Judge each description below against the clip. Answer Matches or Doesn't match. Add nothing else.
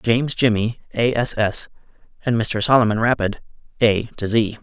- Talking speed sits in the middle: Matches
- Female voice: Doesn't match